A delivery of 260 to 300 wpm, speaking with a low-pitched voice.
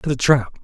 Yes: fast, 285 wpm; low, 130 Hz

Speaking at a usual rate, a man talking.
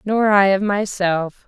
No: average, 165 wpm; female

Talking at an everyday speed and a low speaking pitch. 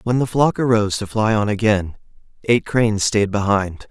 Yes: average, 185 wpm; low, 110 Hz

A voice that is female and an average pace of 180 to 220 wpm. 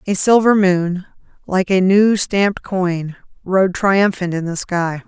No: female; average, 155 wpm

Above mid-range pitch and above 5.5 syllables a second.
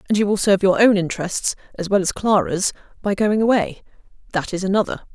Yes: high, 200 Hz; 6.3 syllables/s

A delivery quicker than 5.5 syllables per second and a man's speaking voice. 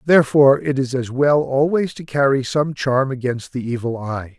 No: 4.9 syllables/s; male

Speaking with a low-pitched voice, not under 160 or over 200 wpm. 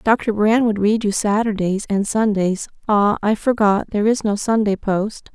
No: high, 210 Hz; average, 170 wpm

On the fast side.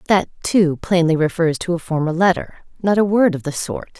No: average, 195 wpm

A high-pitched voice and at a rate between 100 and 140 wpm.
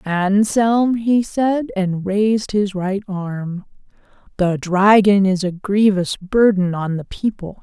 Yes: high, 200 Hz; slow, 135 wpm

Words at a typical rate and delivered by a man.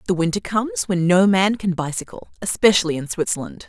No: average, 180 wpm; female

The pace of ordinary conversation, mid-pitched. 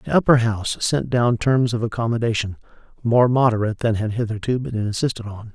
No: average, 175 wpm; low, 115 Hz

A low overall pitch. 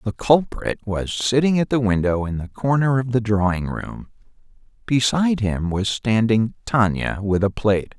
Yes: low, 115 Hz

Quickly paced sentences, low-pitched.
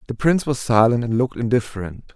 No: average, 195 wpm; low, 120 Hz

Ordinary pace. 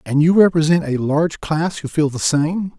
No: fast, 215 wpm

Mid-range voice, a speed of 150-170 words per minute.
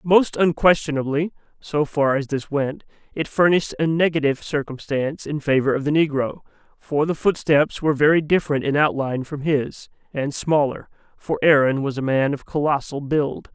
Yes: medium, 150 Hz; average, 165 wpm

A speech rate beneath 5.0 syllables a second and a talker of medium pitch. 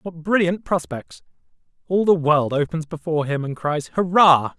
Yes: 4.7 syllables/s; medium, 165 Hz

